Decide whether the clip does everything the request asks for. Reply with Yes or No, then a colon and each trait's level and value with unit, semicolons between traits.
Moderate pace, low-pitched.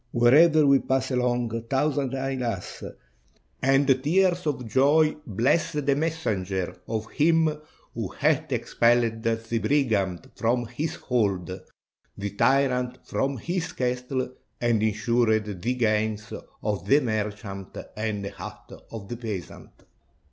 No: slow, 125 wpm; low, 120 Hz